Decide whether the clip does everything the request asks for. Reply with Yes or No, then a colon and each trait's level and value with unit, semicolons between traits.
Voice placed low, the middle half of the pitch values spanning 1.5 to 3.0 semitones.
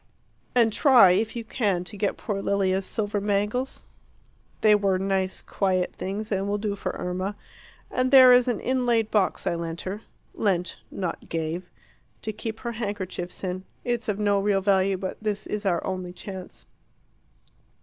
No: high, 200 Hz; narrow, 2.6 semitones